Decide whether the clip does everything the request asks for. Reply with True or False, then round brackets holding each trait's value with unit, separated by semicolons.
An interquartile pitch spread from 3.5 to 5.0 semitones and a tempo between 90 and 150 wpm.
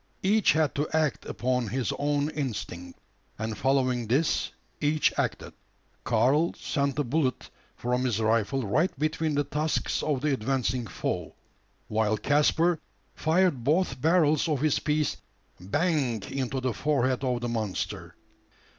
True (4.0 semitones; 135 wpm)